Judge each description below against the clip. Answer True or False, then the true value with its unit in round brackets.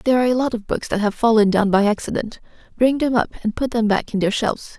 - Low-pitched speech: False (225 Hz)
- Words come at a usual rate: False (275 wpm)